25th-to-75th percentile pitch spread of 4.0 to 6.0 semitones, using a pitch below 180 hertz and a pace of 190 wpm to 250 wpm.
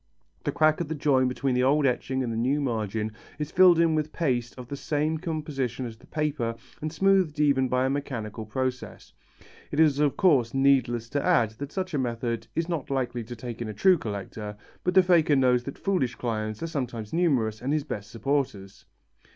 Yes: average, 4.5 semitones; low, 135 Hz; fast, 205 wpm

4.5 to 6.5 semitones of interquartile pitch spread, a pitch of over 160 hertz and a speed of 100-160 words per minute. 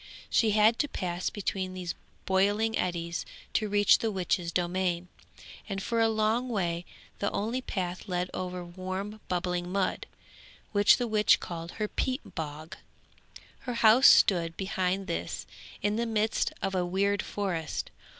No: average, 3.2 semitones; high, 190 Hz; average, 150 wpm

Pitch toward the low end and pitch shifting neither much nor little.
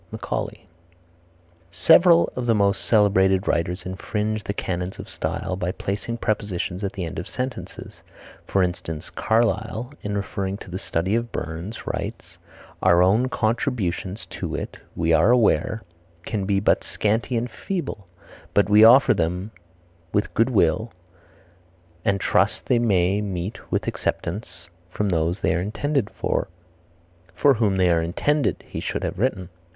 Yes: low, 100 Hz; average, 3.9 semitones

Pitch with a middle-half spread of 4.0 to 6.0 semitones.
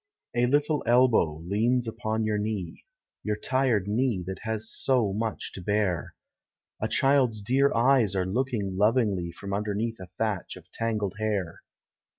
No: average, 3.6 semitones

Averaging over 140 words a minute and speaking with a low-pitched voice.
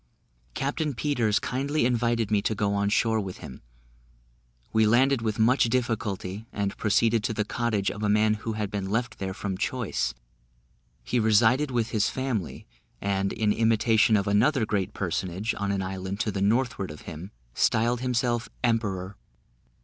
Yes: average, 165 wpm; low, 110 Hz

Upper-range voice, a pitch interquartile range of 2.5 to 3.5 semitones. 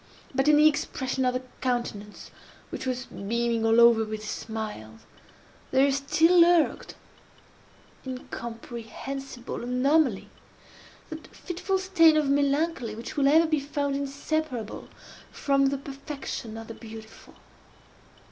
No: very high, 270 Hz; average, 4.3 semitones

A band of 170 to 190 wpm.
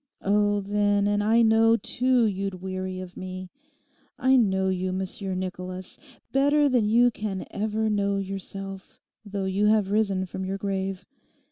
No: average, 150 wpm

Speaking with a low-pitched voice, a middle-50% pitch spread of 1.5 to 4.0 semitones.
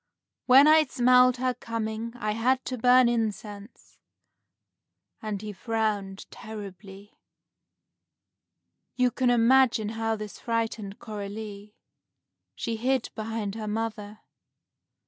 No: high, 225 Hz; average, 2.7 semitones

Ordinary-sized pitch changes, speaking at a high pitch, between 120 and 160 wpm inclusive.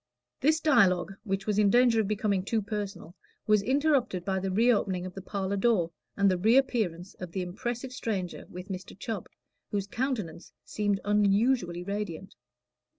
Yes: average, 3.4 semitones; high, 200 Hz; average, 155 wpm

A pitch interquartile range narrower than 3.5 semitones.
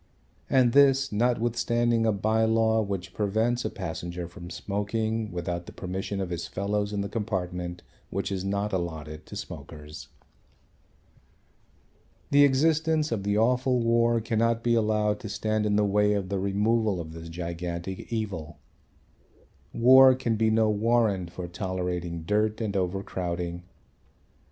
No: average, 4.1 semitones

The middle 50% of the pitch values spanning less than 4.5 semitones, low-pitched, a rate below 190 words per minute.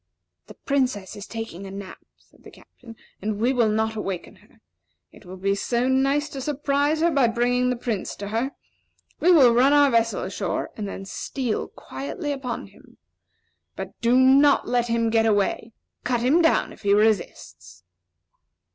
No: average, 4.0 semitones; high, 240 Hz; average, 175 wpm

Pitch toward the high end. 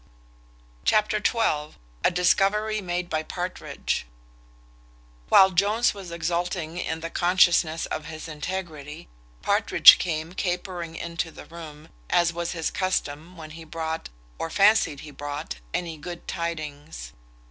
No: medium, 170 Hz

